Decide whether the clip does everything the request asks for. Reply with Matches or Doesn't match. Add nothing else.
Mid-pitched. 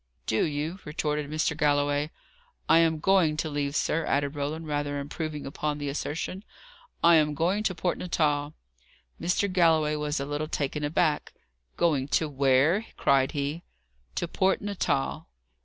Matches